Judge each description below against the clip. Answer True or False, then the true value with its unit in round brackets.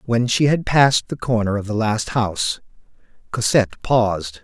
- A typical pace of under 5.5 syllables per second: True (5.0 syllables/s)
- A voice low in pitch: True (115 Hz)